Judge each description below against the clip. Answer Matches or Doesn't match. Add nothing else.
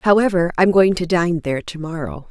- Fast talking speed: Matches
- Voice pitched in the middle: Matches